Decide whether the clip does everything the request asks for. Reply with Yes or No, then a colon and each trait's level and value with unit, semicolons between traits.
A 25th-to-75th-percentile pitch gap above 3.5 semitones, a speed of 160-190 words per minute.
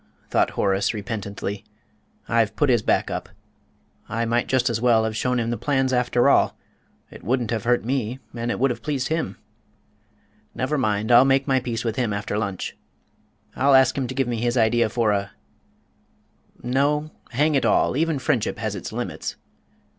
No: average, 3.0 semitones; average, 180 wpm